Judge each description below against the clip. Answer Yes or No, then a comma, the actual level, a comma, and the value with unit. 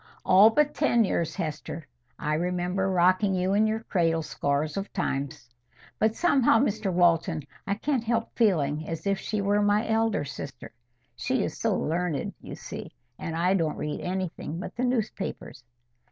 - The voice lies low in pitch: No, medium, 185 Hz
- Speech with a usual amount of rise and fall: Yes, average, 4.9 semitones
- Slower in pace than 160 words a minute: No, average, 165 wpm